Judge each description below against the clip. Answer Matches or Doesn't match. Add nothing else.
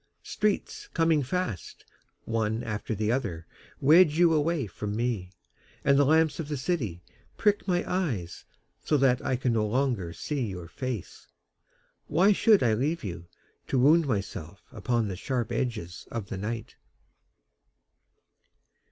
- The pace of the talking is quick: Doesn't match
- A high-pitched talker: Doesn't match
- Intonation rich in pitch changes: Matches